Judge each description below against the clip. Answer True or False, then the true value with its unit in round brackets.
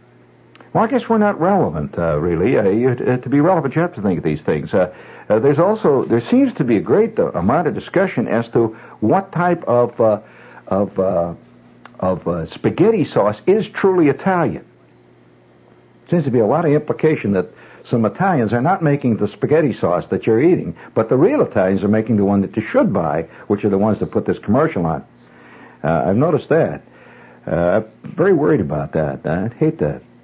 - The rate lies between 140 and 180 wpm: False (200 wpm)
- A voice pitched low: True (105 Hz)